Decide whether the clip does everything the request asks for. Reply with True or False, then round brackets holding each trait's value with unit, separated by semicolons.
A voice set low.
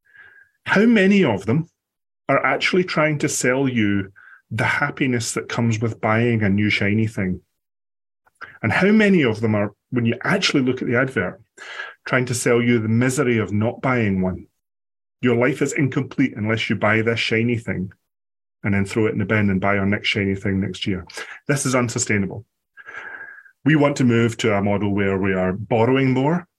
True (115 Hz)